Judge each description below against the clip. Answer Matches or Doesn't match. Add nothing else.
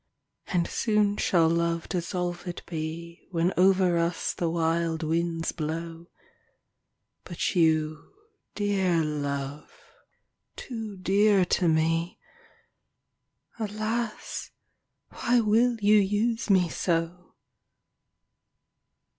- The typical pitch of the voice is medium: Matches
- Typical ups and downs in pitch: Matches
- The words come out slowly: Matches